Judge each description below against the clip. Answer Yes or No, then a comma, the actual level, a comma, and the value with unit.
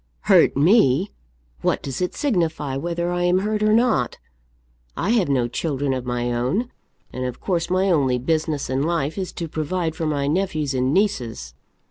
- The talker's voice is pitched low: No, medium, 160 Hz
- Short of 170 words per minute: No, average, 175 wpm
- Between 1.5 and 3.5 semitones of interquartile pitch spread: No, wide, 5.5 semitones